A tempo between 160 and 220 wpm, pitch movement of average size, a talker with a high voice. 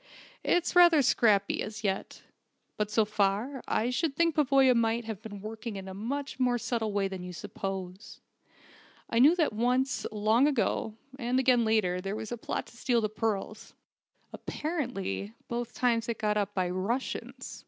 Yes: average, 175 wpm; average, 3.7 semitones; high, 225 Hz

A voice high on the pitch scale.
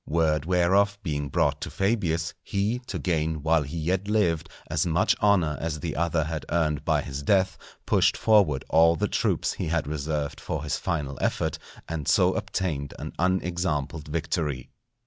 No: very low, 80 Hz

